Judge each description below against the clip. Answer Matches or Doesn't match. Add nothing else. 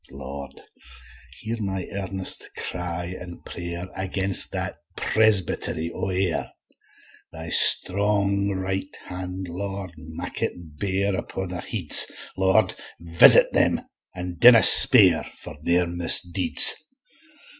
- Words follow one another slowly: Matches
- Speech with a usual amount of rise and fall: Doesn't match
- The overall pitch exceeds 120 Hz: Doesn't match